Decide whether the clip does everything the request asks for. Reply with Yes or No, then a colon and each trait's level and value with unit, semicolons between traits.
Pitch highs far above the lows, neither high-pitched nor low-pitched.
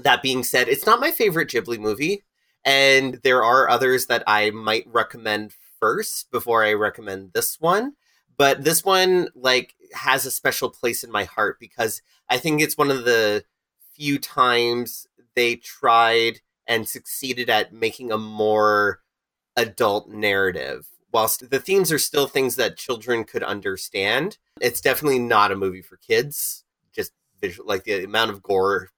No: wide, 6.1 semitones; low, 125 Hz